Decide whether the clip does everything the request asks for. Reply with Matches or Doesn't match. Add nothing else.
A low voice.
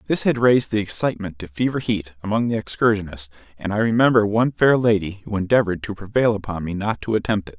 Matches